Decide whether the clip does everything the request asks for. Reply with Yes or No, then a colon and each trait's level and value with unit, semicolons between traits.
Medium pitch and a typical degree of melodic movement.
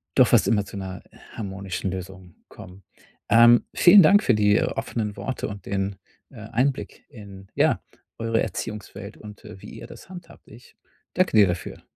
No: low, 105 Hz; average, 3.4 semitones